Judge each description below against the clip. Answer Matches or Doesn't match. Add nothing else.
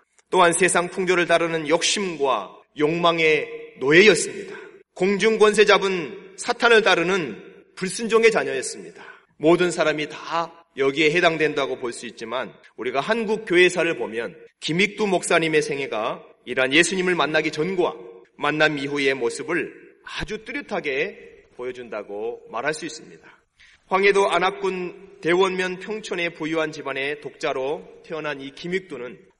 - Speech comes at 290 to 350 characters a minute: Matches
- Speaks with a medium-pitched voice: Matches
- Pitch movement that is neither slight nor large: Doesn't match